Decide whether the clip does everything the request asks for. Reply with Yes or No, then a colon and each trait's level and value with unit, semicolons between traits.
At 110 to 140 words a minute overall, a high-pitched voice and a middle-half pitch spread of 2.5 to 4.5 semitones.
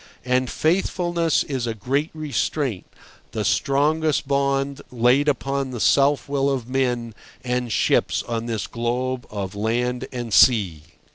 No: slow, 135 wpm; low, 130 Hz; average, 3.0 semitones